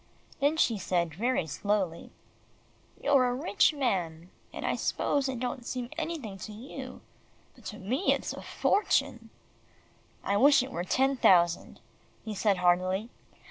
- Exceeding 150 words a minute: No, average, 145 wpm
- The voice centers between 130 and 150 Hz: No, high, 225 Hz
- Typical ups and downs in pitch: No, wide, 6.3 semitones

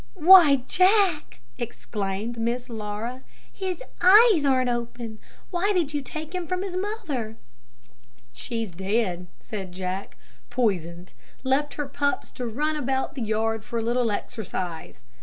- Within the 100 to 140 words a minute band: Yes, slow, 135 wpm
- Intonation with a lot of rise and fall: Yes, wide, 6.3 semitones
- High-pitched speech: Yes, high, 245 Hz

